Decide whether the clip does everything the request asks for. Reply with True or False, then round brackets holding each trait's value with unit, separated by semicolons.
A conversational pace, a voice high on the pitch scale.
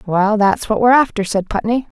False (210 wpm; 220 Hz)